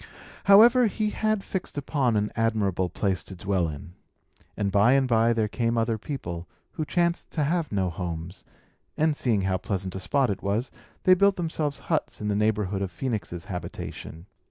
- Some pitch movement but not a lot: No, wide, 7.8 semitones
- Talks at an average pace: Yes, average, 180 wpm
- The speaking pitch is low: Yes, low, 110 Hz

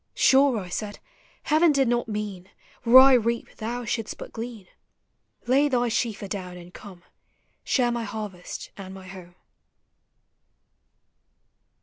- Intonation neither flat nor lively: Yes, average, 4.2 semitones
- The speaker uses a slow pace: Yes, slow, 130 wpm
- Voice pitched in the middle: No, high, 225 Hz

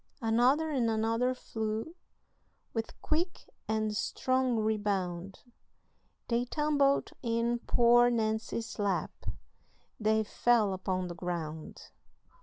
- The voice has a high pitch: Yes, high, 225 Hz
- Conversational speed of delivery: No, slow, 95 wpm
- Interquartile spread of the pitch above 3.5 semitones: No, average, 2.7 semitones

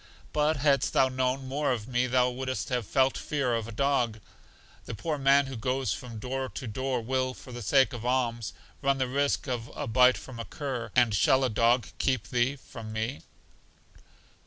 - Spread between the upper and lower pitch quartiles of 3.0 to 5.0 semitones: No, narrow, 2.4 semitones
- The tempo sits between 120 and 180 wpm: No, average, 200 wpm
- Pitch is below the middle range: Yes, low, 125 Hz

